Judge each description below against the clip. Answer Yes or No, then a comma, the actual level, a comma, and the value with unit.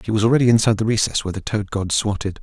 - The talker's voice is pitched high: No, low, 110 Hz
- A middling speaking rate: No, fast, 270 wpm